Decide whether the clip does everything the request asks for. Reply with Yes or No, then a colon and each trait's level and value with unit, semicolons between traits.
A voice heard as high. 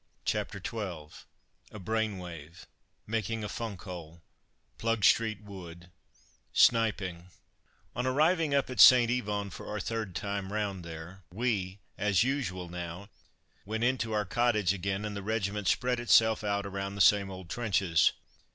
No: low, 100 Hz